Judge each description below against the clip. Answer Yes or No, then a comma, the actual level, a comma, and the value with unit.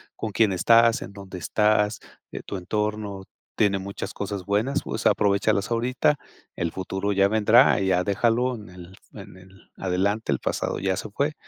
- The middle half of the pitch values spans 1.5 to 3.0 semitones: Yes, narrow, 2.5 semitones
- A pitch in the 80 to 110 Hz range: Yes, low, 100 Hz